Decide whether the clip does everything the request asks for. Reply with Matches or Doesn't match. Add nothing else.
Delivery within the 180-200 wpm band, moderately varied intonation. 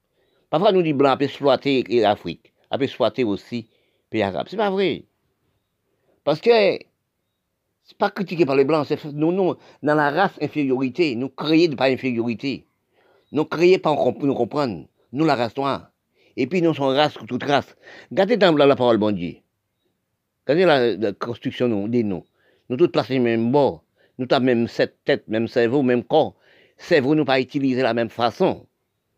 Matches